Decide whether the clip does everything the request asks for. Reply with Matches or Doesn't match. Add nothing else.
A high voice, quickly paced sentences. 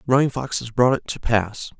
Doesn't match